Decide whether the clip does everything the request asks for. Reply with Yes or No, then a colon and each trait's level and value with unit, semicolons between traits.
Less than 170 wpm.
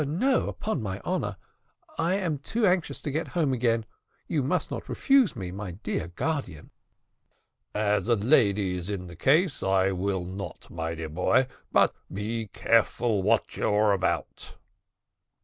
Yes: average, 155 wpm